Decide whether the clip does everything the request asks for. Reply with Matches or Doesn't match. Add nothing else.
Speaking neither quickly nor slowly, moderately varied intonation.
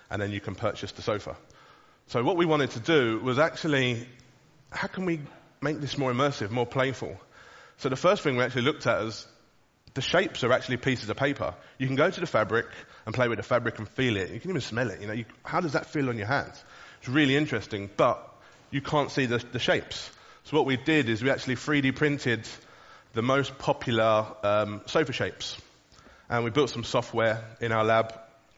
Doesn't match